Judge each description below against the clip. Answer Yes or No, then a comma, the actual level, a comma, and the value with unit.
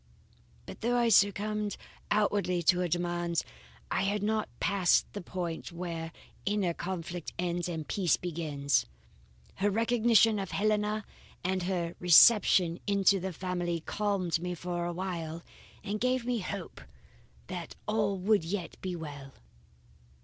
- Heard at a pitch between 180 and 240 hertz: Yes, medium, 185 Hz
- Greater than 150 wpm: No, slow, 135 wpm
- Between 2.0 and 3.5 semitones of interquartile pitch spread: Yes, average, 3.2 semitones